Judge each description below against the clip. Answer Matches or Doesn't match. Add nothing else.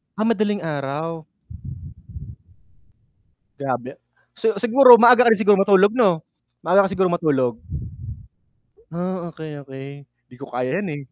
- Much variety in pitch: Matches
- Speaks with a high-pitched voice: Doesn't match